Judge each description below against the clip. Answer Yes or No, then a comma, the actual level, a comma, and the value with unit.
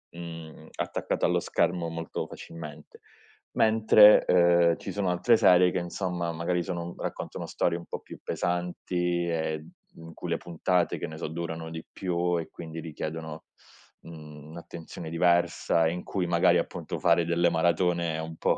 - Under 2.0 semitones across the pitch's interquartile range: Yes, narrow, 1.3 semitones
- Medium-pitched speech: No, very low, 85 Hz